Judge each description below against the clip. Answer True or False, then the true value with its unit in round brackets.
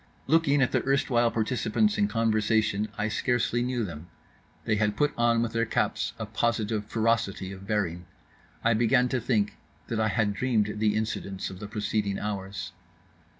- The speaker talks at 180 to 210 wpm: False (165 wpm)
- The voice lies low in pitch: True (110 Hz)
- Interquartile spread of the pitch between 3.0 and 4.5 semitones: False (2.5 semitones)